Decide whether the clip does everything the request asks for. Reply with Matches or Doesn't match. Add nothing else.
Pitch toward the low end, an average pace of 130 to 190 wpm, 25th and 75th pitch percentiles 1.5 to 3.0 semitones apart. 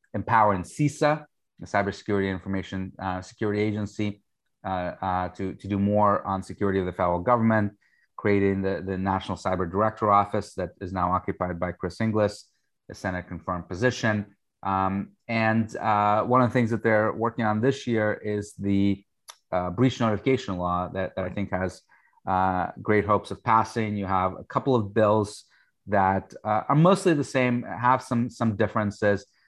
Matches